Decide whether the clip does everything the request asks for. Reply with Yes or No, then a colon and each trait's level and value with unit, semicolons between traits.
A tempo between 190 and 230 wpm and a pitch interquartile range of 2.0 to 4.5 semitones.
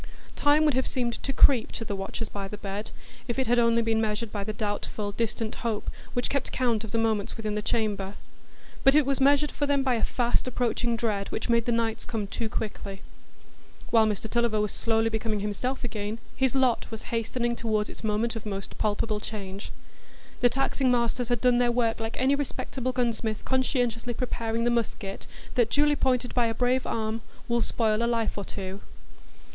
Yes: average, 195 wpm; narrow, 2.5 semitones